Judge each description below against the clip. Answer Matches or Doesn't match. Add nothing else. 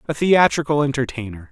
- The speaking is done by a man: Matches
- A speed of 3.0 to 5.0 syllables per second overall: Doesn't match